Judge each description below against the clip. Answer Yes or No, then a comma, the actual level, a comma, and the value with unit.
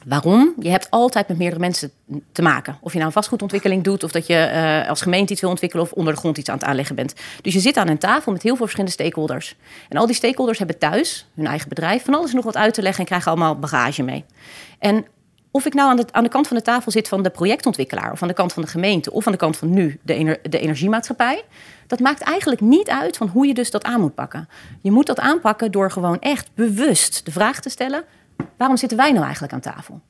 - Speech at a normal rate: No, fast, 260 wpm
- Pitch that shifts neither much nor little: No, wide, 6.7 semitones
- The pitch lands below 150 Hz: No, high, 195 Hz